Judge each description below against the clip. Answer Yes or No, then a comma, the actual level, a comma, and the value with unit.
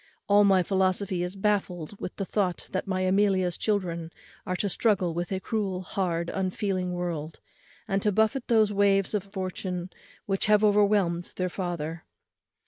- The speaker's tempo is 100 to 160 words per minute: Yes, average, 155 wpm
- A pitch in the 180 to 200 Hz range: Yes, high, 190 Hz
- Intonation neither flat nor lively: No, narrow, 2.3 semitones